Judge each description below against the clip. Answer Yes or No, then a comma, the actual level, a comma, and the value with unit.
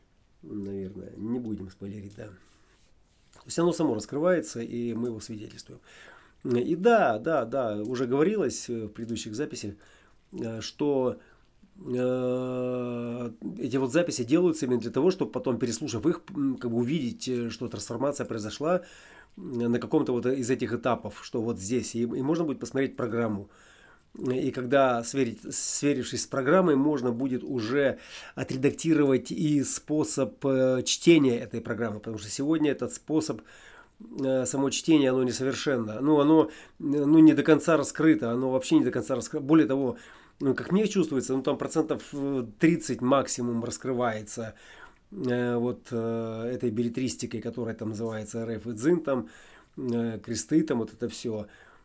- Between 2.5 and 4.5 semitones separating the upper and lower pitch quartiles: Yes, average, 3.6 semitones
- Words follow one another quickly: No, average, 145 wpm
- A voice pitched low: Yes, low, 125 Hz